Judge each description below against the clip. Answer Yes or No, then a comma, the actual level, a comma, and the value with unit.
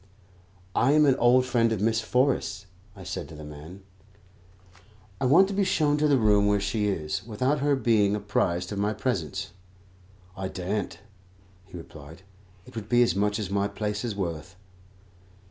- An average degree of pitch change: Yes, average, 4.3 semitones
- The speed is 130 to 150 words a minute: No, average, 175 wpm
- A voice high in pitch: No, low, 105 Hz